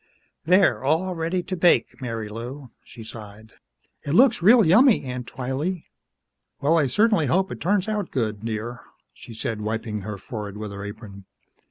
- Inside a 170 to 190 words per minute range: No, average, 160 wpm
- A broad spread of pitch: Yes, wide, 8.7 semitones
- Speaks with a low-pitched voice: Yes, low, 130 Hz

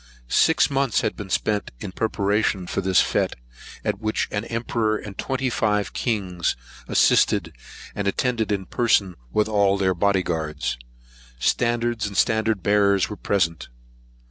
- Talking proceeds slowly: No, average, 145 wpm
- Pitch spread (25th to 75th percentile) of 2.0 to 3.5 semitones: Yes, average, 2.8 semitones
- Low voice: Yes, low, 105 Hz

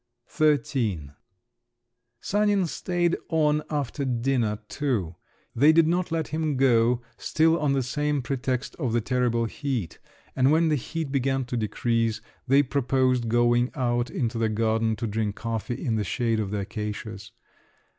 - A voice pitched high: No, low, 125 Hz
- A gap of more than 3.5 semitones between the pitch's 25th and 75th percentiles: Yes, average, 4.4 semitones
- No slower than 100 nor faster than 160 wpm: Yes, average, 150 wpm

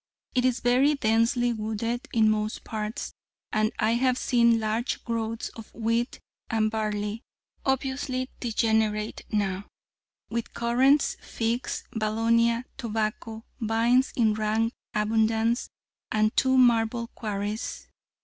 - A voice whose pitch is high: Yes, high, 225 Hz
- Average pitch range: No, narrow, 1.8 semitones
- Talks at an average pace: No, slow, 110 wpm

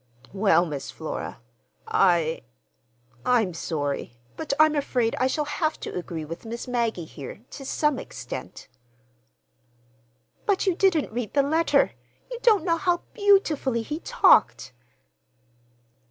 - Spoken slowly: Yes, slow, 125 wpm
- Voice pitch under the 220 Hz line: No, high, 235 Hz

